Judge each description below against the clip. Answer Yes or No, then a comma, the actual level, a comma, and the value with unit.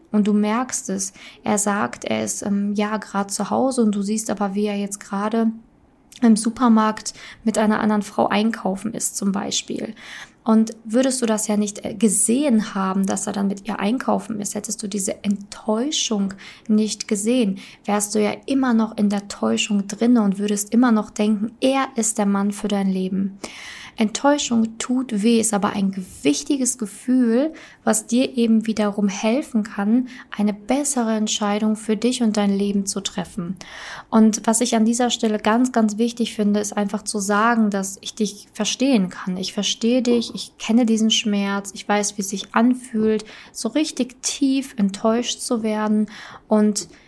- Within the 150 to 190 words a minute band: Yes, average, 175 wpm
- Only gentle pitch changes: Yes, narrow, 2.2 semitones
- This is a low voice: No, high, 215 Hz